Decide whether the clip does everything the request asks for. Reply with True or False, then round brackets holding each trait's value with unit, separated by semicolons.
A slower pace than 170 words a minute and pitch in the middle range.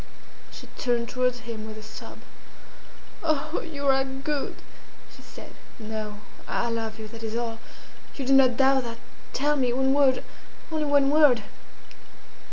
False (155 wpm; 255 Hz)